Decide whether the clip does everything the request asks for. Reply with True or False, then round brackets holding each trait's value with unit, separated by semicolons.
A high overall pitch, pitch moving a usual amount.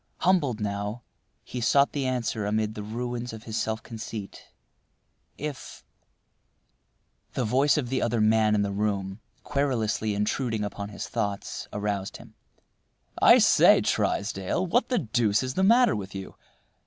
False (110 Hz; 3.9 semitones)